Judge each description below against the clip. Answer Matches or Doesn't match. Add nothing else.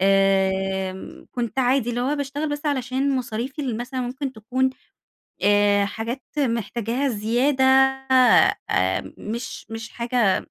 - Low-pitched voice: Doesn't match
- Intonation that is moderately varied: Matches